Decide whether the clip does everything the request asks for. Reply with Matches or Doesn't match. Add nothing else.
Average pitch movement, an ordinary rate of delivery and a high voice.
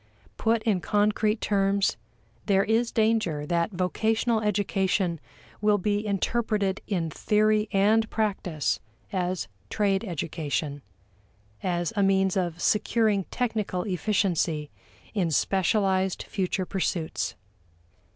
Doesn't match